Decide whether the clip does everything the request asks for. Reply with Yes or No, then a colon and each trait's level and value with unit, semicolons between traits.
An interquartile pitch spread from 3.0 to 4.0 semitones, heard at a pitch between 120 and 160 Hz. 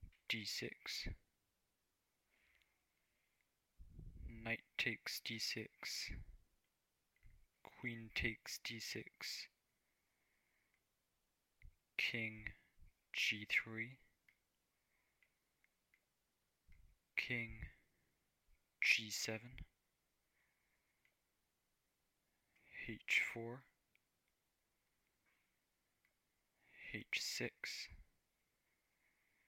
No: average, 3.4 semitones; low, 110 Hz